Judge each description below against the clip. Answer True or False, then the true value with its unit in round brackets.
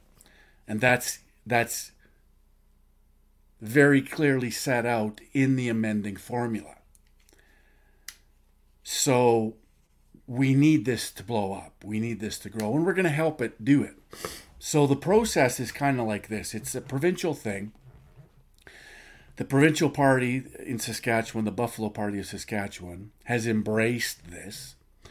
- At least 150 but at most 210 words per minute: False (135 wpm)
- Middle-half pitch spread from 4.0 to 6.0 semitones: True (4.8 semitones)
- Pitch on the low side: True (115 Hz)